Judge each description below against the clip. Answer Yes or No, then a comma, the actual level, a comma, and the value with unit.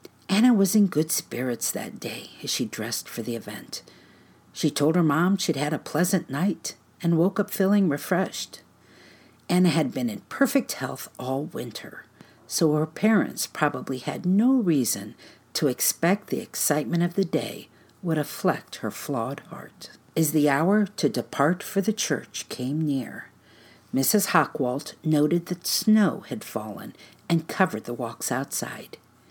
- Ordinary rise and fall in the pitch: No, wide, 6.1 semitones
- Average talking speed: Yes, average, 155 wpm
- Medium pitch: Yes, medium, 155 Hz